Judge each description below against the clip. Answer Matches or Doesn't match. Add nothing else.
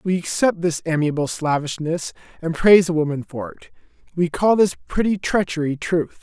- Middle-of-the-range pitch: Matches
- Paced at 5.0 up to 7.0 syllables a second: Matches